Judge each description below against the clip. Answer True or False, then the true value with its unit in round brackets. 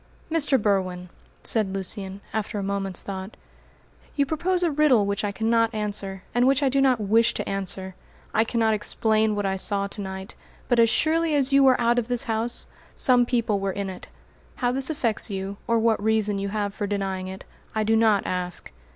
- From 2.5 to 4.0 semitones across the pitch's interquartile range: True (3.6 semitones)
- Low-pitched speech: False (215 Hz)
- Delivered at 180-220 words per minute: True (200 wpm)